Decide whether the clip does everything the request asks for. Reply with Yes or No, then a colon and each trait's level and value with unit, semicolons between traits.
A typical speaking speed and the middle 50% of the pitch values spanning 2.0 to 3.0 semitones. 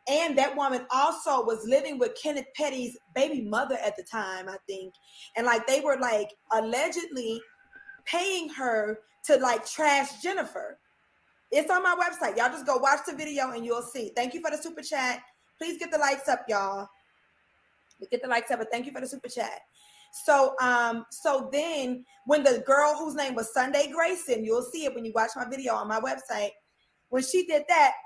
No: average, 195 wpm; average, 4.5 semitones